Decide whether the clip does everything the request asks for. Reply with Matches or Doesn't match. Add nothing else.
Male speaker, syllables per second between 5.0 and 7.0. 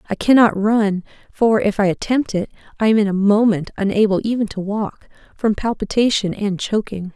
Doesn't match